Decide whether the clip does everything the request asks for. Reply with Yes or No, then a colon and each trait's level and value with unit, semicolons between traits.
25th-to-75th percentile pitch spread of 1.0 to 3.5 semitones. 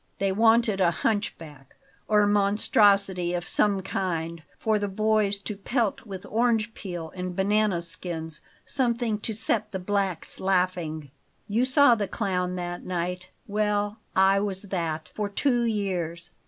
Yes: average, 3.1 semitones